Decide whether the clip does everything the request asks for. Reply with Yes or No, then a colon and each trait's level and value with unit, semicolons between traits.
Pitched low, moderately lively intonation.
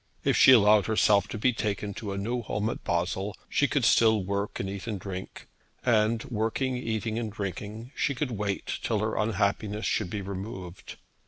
No: low, 105 Hz; narrow, 2.2 semitones